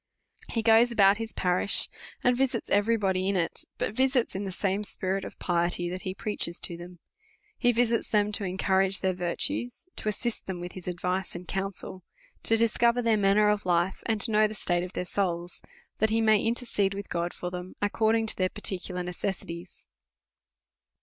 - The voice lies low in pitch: No, high, 195 Hz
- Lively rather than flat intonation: No, average, 3.5 semitones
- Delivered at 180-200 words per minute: Yes, average, 190 wpm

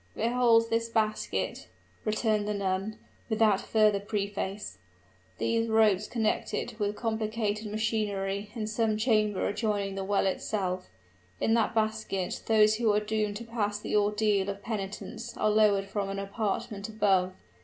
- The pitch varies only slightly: Yes, narrow, 1.6 semitones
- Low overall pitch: No, high, 210 Hz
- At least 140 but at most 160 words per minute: Yes, average, 145 wpm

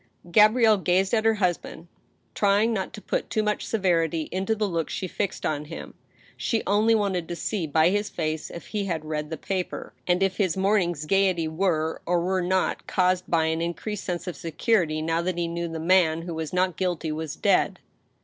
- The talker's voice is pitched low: No, medium, 180 Hz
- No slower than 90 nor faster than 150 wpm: No, average, 200 wpm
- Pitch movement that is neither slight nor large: Yes, average, 3.3 semitones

